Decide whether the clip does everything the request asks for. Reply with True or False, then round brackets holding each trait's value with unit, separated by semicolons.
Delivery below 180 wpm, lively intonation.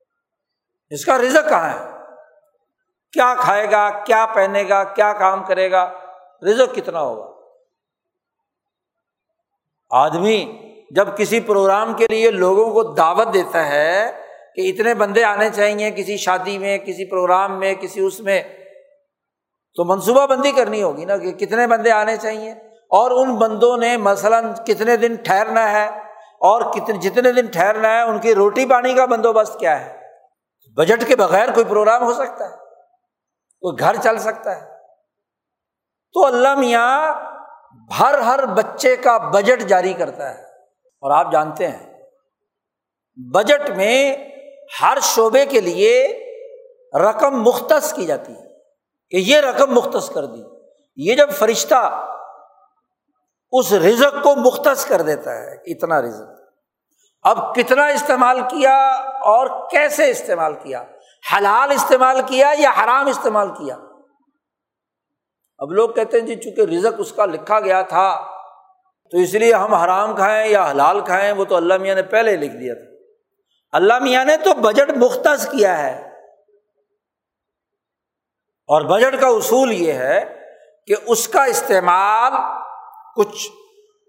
True (140 wpm; 5.7 semitones)